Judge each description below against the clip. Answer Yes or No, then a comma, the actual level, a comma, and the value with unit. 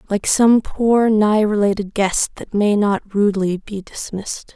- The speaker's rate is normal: Yes, average, 160 wpm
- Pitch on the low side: No, high, 205 Hz